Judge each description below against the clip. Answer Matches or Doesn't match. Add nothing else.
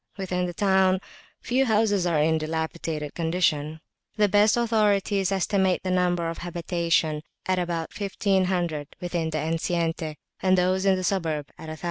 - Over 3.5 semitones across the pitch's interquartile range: Doesn't match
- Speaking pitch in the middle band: Matches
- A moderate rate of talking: Matches